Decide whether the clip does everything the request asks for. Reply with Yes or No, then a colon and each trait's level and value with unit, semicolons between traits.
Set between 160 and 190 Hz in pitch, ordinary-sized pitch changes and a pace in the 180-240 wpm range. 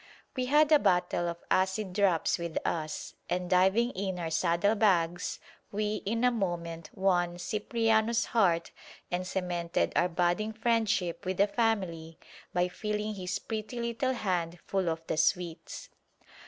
No: medium, 185 Hz; average, 3.8 semitones; average, 145 wpm